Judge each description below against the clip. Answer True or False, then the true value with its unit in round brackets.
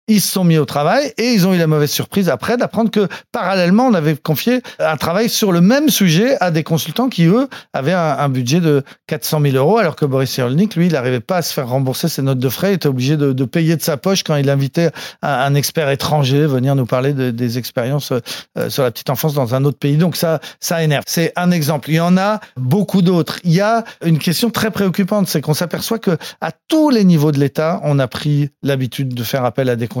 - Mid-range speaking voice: True (160 Hz)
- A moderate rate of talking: False (250 wpm)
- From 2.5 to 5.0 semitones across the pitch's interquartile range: False (5.4 semitones)